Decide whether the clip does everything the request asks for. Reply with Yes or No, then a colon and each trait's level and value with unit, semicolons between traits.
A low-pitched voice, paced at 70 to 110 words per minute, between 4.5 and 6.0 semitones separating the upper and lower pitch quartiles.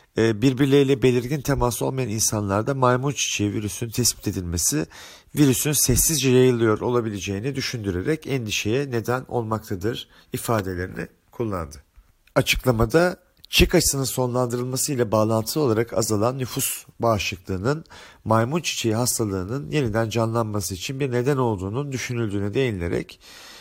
No: low, 120 Hz; average, 105 wpm; average, 4.1 semitones